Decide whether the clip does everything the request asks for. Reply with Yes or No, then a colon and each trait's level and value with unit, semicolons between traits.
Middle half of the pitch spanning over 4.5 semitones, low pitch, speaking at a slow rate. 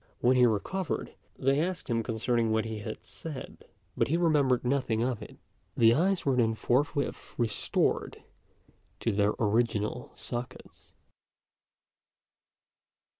No: average, 3.8 semitones; low, 120 Hz; slow, 125 wpm